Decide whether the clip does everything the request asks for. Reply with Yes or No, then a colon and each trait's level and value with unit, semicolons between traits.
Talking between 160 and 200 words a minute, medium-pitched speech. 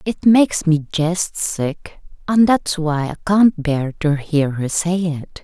Yes: average, 175 wpm; medium, 165 Hz